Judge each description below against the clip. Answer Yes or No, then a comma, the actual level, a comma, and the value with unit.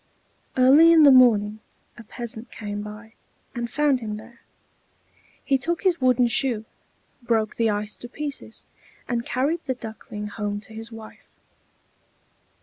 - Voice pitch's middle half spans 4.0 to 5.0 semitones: No, average, 3.3 semitones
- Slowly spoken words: No, average, 145 wpm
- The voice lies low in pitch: No, high, 235 Hz